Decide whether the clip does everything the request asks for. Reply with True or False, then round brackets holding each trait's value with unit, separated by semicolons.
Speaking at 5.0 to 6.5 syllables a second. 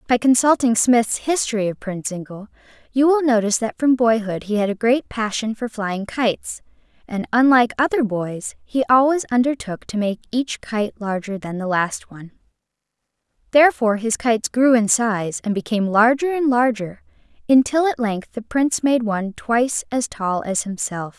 True (5.1 syllables/s)